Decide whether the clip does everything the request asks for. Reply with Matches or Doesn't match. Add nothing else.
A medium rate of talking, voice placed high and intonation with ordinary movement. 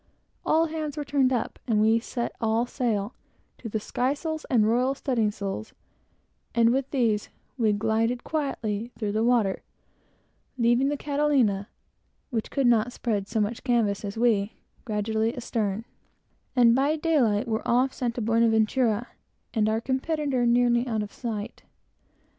Matches